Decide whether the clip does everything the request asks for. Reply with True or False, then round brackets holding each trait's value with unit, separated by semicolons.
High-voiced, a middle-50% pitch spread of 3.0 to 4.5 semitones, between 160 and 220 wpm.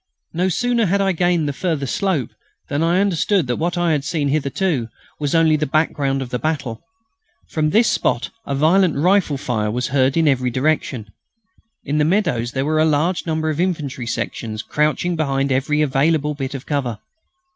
False (150 Hz; 3.8 semitones; 180 wpm)